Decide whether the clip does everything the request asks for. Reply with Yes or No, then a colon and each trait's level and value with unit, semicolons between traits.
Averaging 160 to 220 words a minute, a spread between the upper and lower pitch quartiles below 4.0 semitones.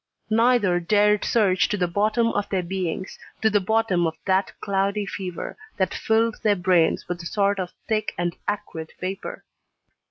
Yes: average, 165 wpm; average, 2.9 semitones